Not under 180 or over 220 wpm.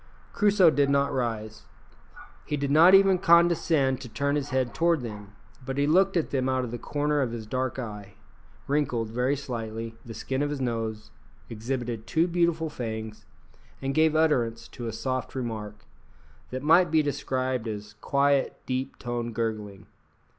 No: average, 165 wpm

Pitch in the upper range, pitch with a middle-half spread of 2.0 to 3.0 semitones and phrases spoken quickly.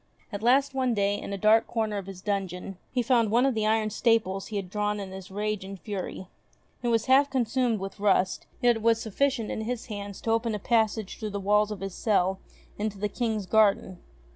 Yes: high, 215 Hz; narrow, 2.6 semitones; fast, 220 wpm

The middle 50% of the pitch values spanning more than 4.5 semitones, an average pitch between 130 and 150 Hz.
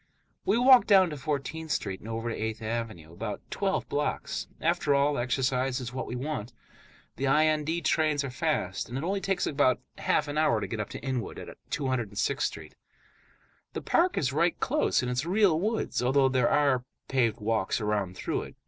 Yes: average, 4.9 semitones; low, 135 Hz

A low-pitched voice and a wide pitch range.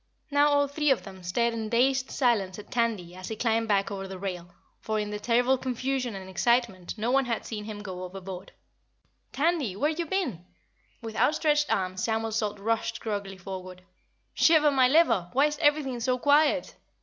No: high, 230 Hz; wide, 5.7 semitones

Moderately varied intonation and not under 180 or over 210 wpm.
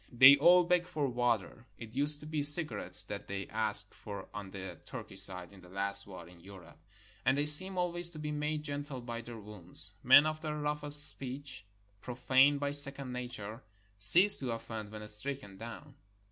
No: wide, 6.0 semitones; average, 190 wpm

